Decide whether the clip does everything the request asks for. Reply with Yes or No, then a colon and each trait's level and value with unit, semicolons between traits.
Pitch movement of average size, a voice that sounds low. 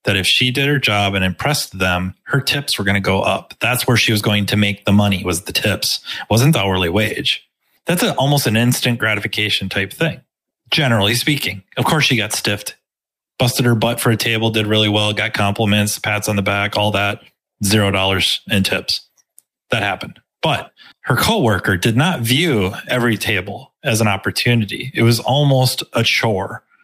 Yes: average, 3.7 semitones; low, 110 Hz